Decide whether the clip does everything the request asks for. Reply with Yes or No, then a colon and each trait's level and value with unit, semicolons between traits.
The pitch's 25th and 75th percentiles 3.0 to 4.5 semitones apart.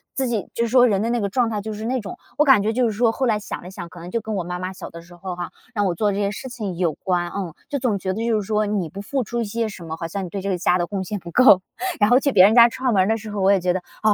Yes: average, 3.9 semitones